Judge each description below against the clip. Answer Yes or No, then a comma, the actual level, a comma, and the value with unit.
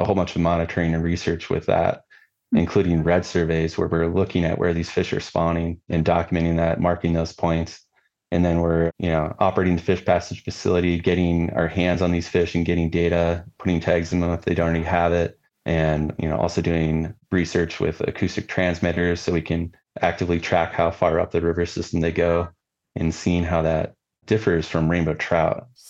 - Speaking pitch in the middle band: No, very low, 85 Hz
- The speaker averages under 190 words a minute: No, average, 200 wpm